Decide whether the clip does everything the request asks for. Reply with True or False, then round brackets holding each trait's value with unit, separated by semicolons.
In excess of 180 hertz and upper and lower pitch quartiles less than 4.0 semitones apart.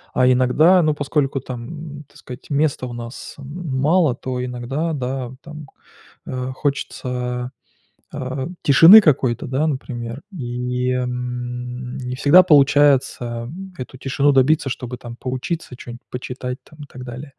False (130 Hz; 2.8 semitones)